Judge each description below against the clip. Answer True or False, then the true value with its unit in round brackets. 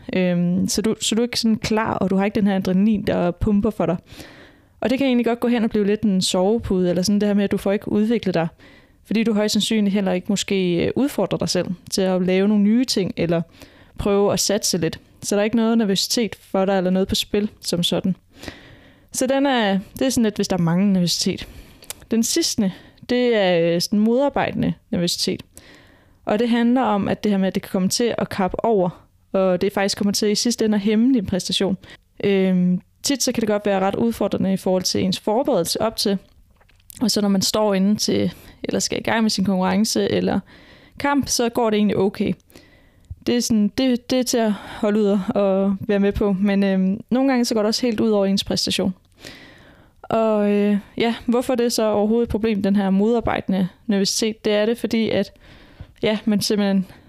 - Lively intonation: False (2.9 semitones)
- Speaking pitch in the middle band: False (205 Hz)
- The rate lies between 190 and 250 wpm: True (220 wpm)